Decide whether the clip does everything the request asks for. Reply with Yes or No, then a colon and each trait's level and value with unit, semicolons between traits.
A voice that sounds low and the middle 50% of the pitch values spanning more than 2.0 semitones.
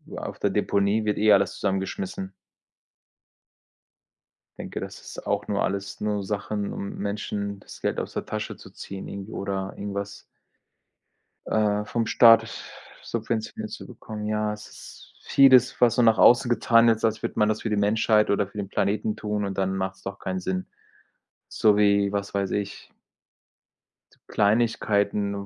No: low, 105 Hz; narrow, 1.5 semitones